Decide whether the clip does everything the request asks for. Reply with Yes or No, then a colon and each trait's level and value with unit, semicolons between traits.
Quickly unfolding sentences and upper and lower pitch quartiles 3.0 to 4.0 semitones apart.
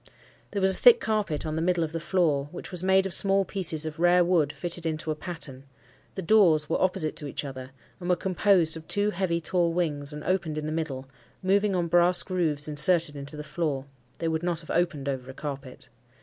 Yes: fast, 220 wpm; average, 3.5 semitones